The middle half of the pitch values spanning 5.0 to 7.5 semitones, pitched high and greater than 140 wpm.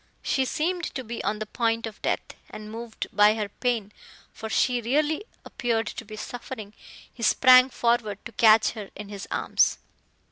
No: narrow, 2.6 semitones; high, 230 Hz; average, 175 wpm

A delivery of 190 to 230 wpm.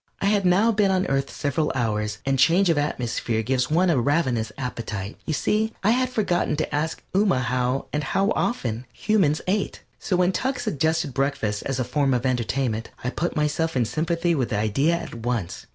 Yes: average, 195 wpm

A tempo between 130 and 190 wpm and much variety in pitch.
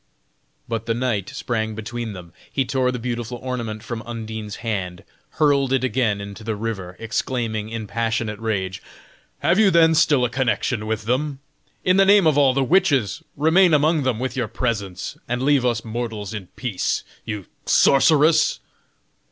No: average, 165 wpm; average, 3.7 semitones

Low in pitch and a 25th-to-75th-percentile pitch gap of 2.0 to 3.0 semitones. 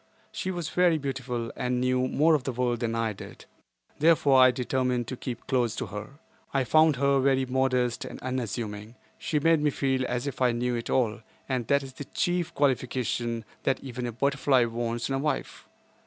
Yes: low, 130 Hz; narrow, 2.5 semitones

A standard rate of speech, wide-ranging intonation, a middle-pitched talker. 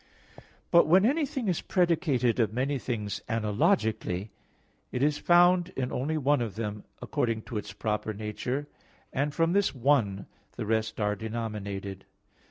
No: average, 145 wpm; wide, 6.7 semitones; low, 120 Hz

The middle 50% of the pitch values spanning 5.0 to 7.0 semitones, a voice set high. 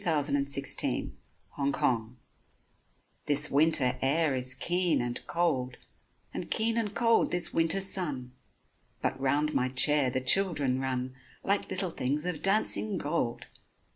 No: average, 5.3 semitones; medium, 145 Hz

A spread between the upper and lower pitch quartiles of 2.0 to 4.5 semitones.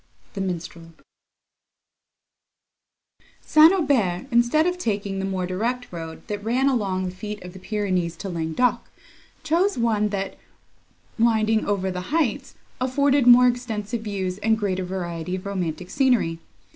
No: average, 5.1 semitones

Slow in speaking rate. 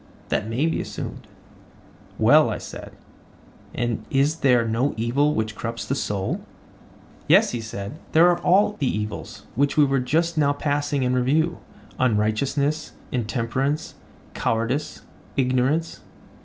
Yes: slow, 130 wpm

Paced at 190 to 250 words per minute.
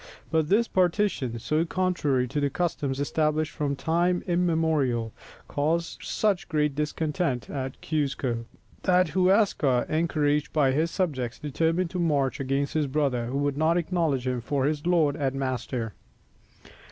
No: average, 140 wpm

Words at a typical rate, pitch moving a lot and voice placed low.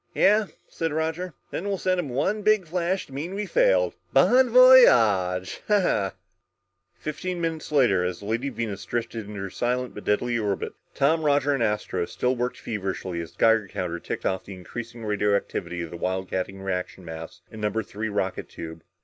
Yes: average, 175 wpm; wide, 8.9 semitones; low, 115 Hz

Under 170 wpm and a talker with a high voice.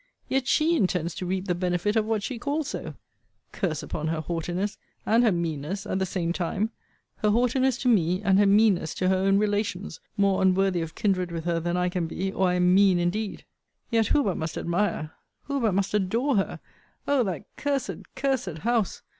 No: average, 200 wpm; high, 195 Hz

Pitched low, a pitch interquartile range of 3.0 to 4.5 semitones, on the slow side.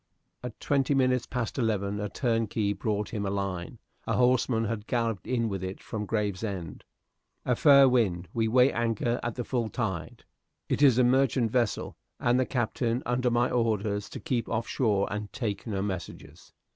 No: low, 115 Hz; average, 3.3 semitones; average, 175 wpm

